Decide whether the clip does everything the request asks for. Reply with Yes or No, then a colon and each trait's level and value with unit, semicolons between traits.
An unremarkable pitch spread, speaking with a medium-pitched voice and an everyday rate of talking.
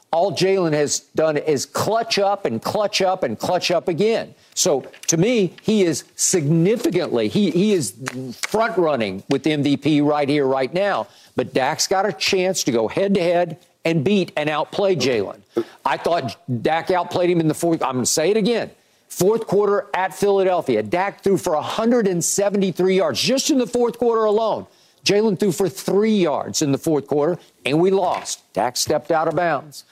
Yes: average, 4.4 semitones; medium, 180 Hz; average, 180 wpm